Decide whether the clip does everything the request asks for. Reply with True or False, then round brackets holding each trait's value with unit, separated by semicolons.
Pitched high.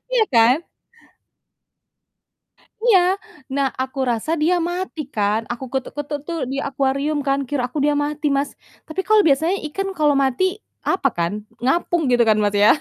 True (285 Hz)